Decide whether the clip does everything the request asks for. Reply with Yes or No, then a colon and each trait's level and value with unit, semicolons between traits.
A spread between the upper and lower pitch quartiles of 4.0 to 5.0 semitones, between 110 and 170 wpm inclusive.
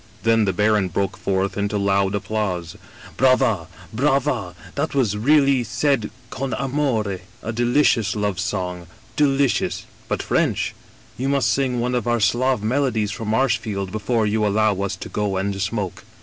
Yes: average, 4.5 semitones; average, 165 wpm